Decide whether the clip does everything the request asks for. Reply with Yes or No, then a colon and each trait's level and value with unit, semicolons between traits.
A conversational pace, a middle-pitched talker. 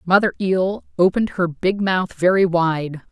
Yes: average, 155 wpm; medium, 165 Hz